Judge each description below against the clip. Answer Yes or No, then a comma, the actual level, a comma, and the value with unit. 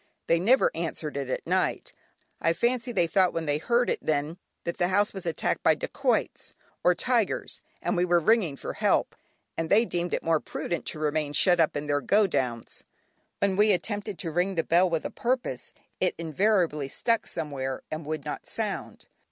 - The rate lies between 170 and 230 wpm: Yes, average, 195 wpm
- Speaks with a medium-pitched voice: Yes, medium, 170 Hz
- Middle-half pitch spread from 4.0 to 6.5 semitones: Yes, average, 4.6 semitones